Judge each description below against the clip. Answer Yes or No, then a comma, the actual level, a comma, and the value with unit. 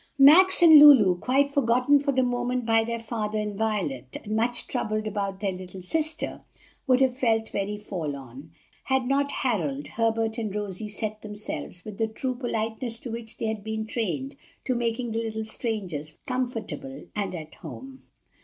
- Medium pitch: No, high, 220 Hz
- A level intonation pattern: No, average, 3.7 semitones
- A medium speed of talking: Yes, average, 170 wpm